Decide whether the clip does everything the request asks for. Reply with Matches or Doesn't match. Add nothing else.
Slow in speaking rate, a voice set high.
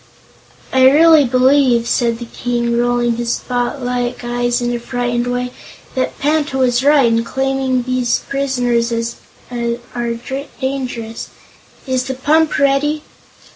Matches